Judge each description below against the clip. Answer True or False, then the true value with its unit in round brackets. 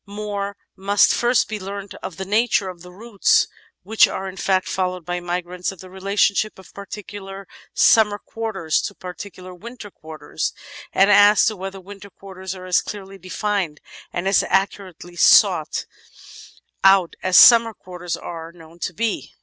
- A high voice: True (195 Hz)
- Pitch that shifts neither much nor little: False (2.1 semitones)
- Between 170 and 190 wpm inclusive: False (160 wpm)